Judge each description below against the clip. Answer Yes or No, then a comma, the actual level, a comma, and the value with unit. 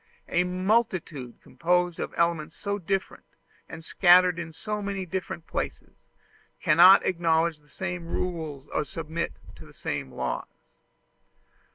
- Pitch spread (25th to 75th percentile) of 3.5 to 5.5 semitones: No, narrow, 2.5 semitones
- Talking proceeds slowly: Yes, slow, 130 wpm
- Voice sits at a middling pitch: Yes, medium, 170 Hz